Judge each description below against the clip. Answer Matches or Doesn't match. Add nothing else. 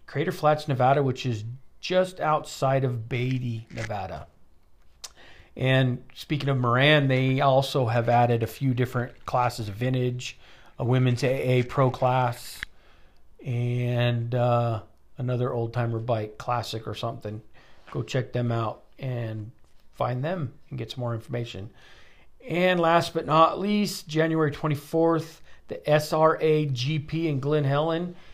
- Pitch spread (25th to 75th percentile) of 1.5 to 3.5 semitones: Doesn't match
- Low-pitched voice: Matches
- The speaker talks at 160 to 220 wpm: Doesn't match